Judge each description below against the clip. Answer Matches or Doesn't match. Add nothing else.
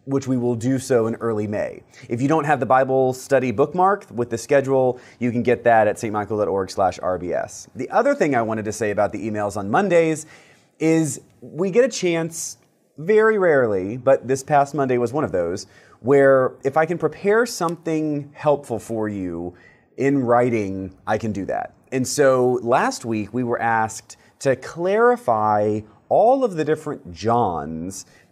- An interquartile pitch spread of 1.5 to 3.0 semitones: Doesn't match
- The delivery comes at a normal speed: Matches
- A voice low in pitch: Matches